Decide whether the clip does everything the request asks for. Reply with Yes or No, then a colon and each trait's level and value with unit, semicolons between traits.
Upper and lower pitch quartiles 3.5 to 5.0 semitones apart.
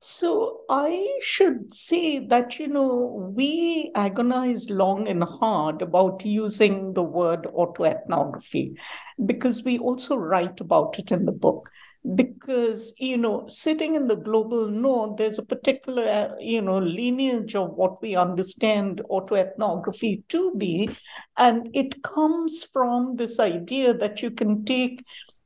Yes: average, 4.4 semitones